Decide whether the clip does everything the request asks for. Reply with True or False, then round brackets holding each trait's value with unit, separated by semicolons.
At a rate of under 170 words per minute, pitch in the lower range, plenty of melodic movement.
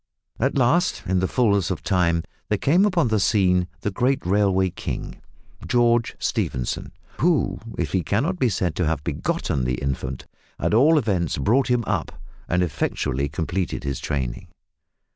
True (160 wpm; 95 Hz; 6.4 semitones)